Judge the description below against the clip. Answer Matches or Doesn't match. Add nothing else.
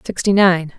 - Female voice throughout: Matches